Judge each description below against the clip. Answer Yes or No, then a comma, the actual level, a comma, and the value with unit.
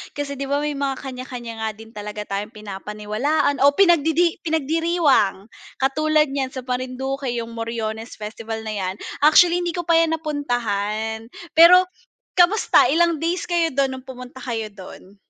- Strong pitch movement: Yes, wide, 5.8 semitones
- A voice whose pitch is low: No, very high, 265 Hz